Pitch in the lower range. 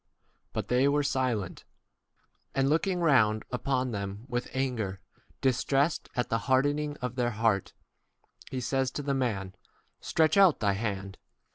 Yes: low, 125 Hz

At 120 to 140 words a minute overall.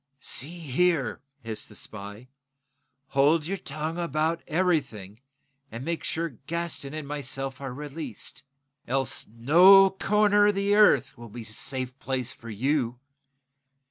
Yes: slow, 135 wpm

